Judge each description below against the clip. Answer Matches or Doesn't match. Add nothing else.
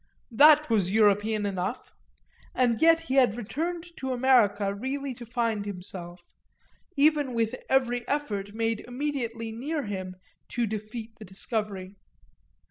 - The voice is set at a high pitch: Matches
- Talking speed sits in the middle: Doesn't match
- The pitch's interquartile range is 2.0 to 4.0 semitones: Doesn't match